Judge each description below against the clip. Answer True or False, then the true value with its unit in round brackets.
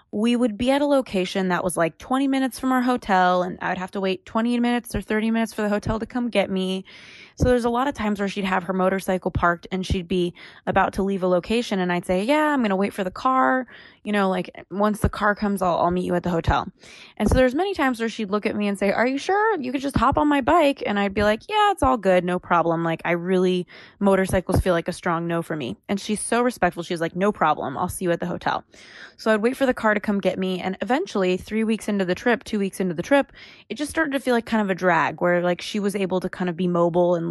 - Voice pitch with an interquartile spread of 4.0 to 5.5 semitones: True (4.7 semitones)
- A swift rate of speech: True (280 wpm)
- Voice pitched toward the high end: True (200 Hz)